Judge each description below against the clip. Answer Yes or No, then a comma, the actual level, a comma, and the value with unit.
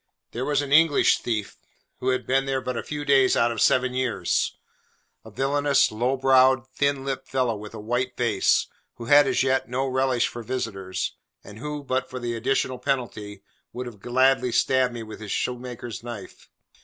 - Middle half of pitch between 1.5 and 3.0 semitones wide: Yes, narrow, 2.4 semitones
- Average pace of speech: Yes, average, 185 wpm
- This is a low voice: Yes, low, 125 Hz